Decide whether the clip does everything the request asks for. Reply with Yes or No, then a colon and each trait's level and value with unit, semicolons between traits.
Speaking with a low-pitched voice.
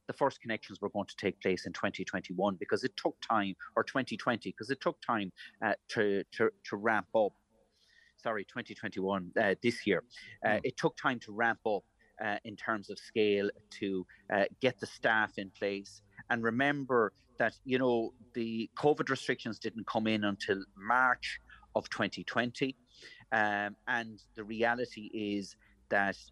Yes: low, 110 Hz